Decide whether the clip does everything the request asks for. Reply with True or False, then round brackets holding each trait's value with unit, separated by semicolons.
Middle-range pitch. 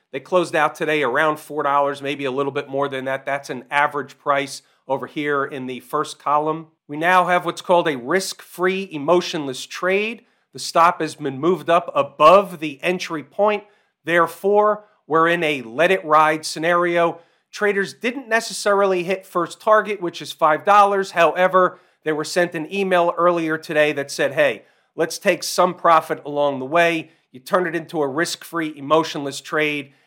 True (165 Hz)